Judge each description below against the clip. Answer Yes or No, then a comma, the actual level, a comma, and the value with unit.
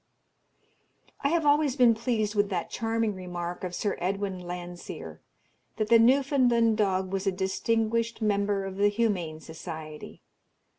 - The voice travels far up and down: No, average, 3.9 semitones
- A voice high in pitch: Yes, high, 205 Hz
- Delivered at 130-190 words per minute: Yes, average, 140 wpm